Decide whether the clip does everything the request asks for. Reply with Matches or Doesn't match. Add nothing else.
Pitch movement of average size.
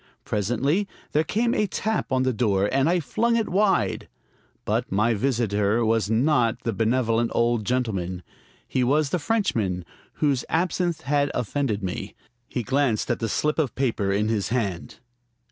Doesn't match